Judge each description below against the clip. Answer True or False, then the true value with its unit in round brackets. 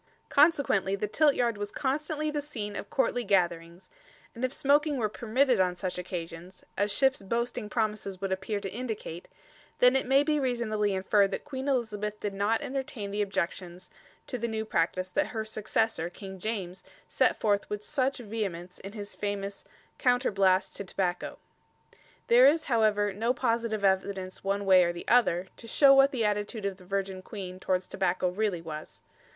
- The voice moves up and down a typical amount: True (4.3 semitones)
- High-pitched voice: True (210 Hz)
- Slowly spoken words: False (170 wpm)